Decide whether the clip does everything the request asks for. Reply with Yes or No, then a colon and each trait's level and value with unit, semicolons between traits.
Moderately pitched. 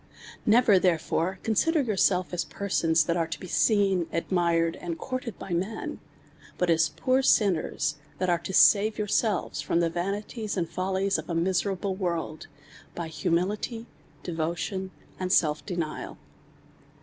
Yes: medium, 180 Hz